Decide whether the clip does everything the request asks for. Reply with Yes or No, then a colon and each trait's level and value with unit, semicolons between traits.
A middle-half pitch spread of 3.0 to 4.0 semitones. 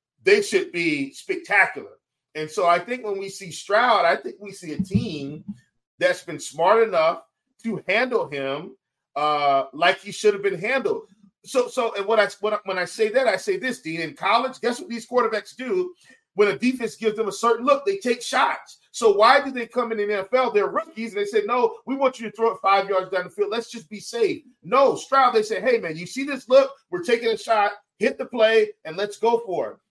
No: wide, 5.6 semitones